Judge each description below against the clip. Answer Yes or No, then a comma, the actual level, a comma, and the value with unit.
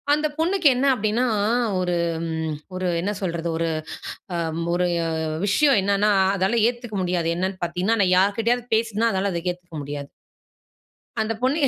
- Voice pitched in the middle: No, high, 195 Hz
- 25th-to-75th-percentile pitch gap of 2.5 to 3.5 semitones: No, average, 4.7 semitones